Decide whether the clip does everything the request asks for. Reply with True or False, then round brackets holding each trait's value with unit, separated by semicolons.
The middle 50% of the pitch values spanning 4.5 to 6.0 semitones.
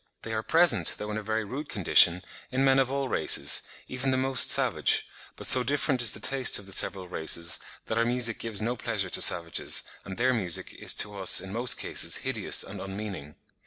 True (5.0 semitones)